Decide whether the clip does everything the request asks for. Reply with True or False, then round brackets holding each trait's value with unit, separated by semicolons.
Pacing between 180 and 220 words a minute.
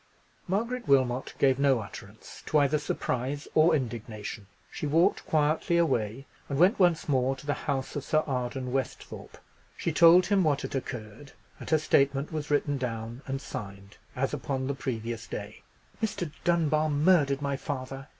False (160 wpm)